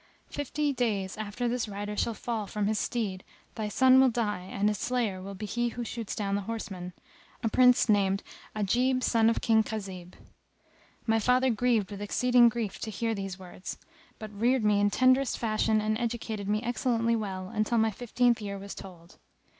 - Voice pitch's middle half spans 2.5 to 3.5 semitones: Yes, average, 3.0 semitones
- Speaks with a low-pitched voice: No, high, 220 Hz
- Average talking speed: Yes, average, 185 wpm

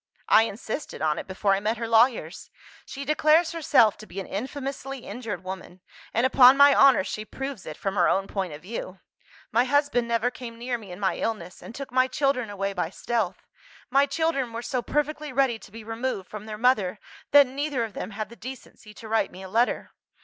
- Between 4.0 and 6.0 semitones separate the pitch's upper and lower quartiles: Yes, average, 5.1 semitones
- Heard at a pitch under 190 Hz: No, high, 230 Hz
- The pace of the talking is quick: Yes, fast, 210 wpm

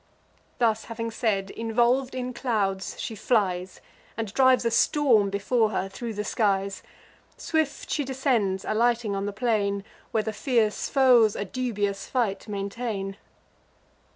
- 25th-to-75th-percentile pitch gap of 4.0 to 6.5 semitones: No, average, 3.6 semitones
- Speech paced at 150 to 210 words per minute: No, slow, 135 wpm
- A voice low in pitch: No, high, 220 Hz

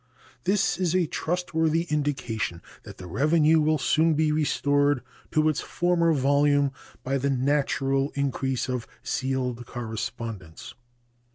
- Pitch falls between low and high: Yes, medium, 145 Hz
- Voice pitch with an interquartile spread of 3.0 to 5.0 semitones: Yes, average, 3.4 semitones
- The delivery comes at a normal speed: No, slow, 120 wpm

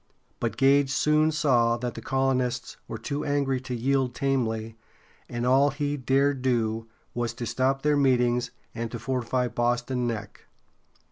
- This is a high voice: No, low, 125 Hz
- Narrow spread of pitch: Yes, narrow, 2.3 semitones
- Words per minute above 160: No, average, 150 wpm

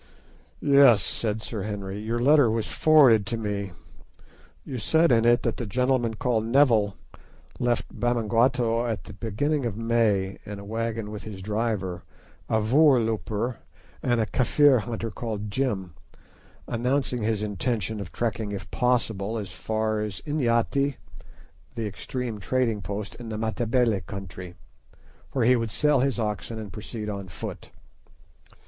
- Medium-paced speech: Yes, average, 145 wpm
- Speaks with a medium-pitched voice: No, low, 115 Hz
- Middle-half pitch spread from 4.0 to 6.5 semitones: No, average, 2.8 semitones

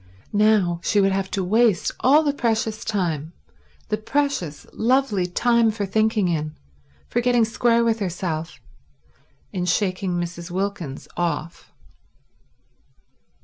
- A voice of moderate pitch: No, high, 200 Hz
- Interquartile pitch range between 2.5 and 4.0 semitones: No, average, 4.5 semitones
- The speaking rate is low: Yes, slow, 120 wpm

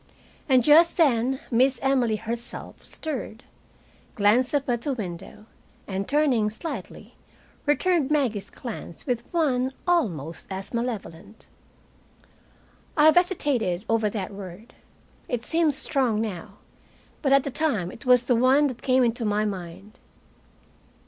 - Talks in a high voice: Yes, high, 240 Hz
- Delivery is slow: Yes, slow, 130 wpm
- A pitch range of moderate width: Yes, average, 4.7 semitones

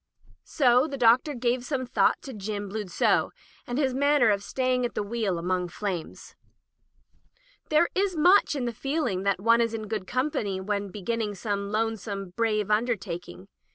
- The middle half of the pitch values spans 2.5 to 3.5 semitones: No, average, 4.1 semitones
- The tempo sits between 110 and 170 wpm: Yes, average, 165 wpm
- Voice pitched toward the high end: Yes, high, 225 Hz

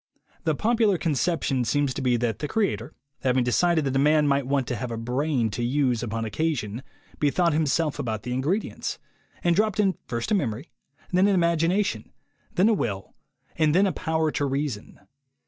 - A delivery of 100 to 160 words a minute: No, average, 185 wpm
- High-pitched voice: No, medium, 145 Hz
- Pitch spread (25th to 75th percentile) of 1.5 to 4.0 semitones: No, wide, 5.6 semitones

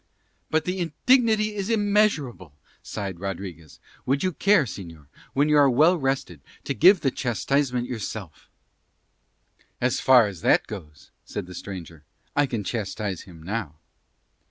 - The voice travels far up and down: Yes, wide, 8.8 semitones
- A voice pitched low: Yes, low, 125 Hz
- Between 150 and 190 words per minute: No, average, 140 wpm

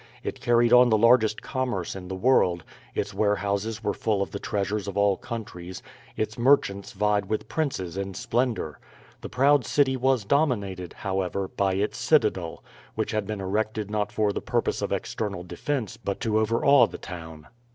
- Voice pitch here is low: Yes, low, 105 Hz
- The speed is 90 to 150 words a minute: No, average, 170 wpm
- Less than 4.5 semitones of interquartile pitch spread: Yes, average, 3.5 semitones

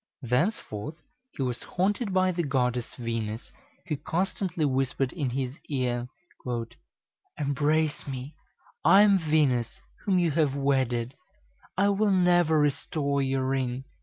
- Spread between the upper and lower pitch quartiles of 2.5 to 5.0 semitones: No, wide, 5.4 semitones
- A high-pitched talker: No, medium, 140 Hz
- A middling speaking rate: No, slow, 125 wpm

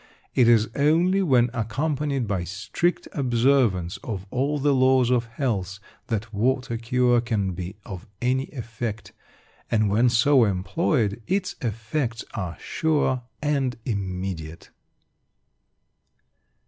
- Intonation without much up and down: No, average, 4.7 semitones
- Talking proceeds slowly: Yes, slow, 115 wpm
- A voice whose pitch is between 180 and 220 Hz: No, low, 120 Hz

